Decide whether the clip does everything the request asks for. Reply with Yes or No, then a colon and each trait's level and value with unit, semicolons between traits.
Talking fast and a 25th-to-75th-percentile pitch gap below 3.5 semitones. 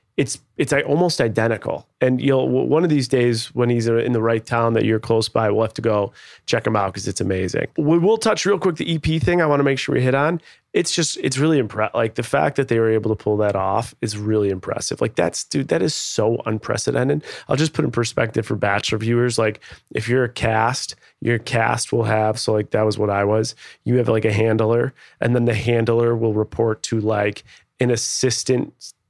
Yes: fast, 225 wpm; average, 2.9 semitones